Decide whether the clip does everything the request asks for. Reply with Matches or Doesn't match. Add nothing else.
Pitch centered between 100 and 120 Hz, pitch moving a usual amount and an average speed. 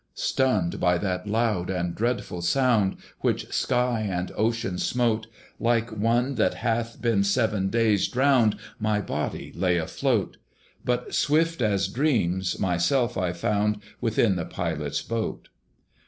Doesn't match